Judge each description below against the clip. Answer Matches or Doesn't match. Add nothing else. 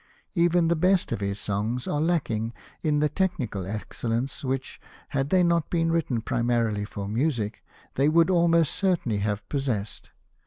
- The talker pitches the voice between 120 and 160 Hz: Matches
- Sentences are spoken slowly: Doesn't match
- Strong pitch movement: Matches